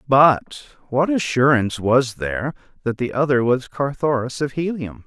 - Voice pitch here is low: Yes, low, 130 Hz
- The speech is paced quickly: No, average, 140 wpm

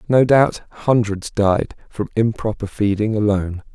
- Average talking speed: No, slow, 130 wpm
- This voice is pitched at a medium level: No, low, 110 Hz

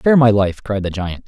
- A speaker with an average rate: No, fast, 280 wpm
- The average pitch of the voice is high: No, low, 105 Hz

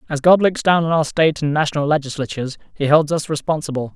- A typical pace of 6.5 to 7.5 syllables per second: Yes, 6.7 syllables/s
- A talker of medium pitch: Yes, medium, 150 Hz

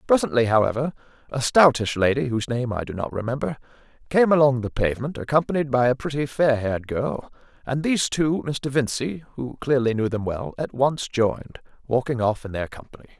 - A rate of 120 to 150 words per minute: No, average, 180 wpm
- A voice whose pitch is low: Yes, low, 130 Hz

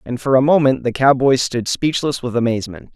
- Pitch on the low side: Yes, low, 130 Hz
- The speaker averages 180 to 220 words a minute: Yes, fast, 205 wpm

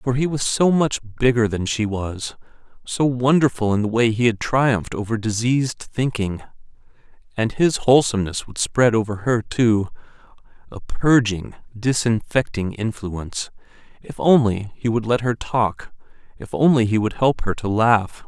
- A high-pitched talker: No, low, 115 Hz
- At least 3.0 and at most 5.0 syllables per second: Yes, 4.6 syllables/s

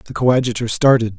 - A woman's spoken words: No, male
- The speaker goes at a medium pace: Yes, average, 150 wpm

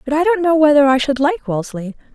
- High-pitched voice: Yes, very high, 285 Hz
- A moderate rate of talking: No, fast, 250 wpm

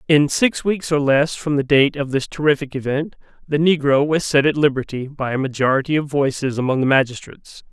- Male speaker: Yes, male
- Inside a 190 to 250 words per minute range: Yes, average, 200 wpm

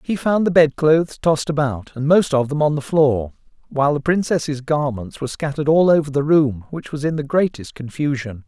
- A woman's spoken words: No, male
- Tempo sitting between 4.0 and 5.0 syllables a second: No, 5.5 syllables/s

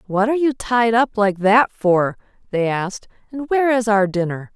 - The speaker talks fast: No, average, 195 wpm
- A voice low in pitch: No, high, 220 Hz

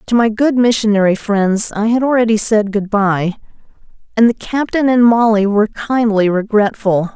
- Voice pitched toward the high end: Yes, high, 220 Hz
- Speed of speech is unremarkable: Yes, average, 160 wpm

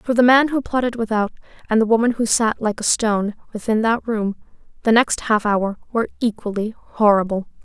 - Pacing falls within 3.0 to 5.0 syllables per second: No, 5.4 syllables/s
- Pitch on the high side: Yes, high, 220 Hz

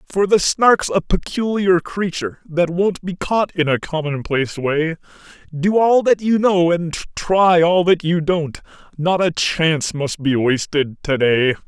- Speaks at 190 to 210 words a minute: No, average, 170 wpm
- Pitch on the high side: No, medium, 170 Hz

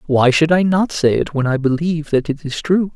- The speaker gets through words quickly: Yes, fast, 265 wpm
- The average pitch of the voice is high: No, medium, 155 Hz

